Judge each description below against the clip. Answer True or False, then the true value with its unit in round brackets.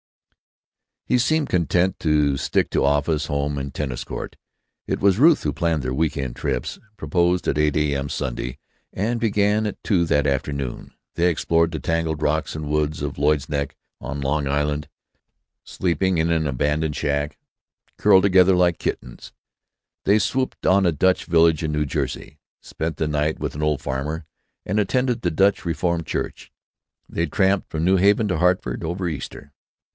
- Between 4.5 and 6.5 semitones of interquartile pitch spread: False (4.0 semitones)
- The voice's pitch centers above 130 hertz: False (80 Hz)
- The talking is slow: False (170 wpm)